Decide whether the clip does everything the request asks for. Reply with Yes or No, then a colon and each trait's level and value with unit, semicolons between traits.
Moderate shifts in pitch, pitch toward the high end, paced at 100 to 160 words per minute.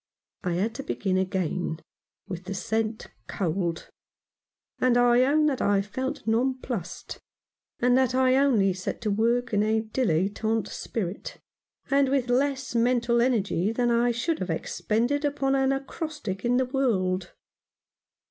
Yes: average, 4.8 semitones; high, 235 Hz; average, 140 wpm